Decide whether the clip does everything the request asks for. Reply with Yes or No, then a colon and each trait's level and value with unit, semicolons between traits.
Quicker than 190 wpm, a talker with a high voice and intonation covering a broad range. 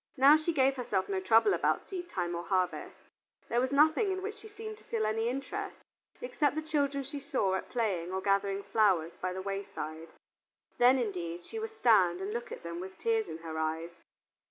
Yes: average, 200 wpm; high, 225 Hz; wide, 8.4 semitones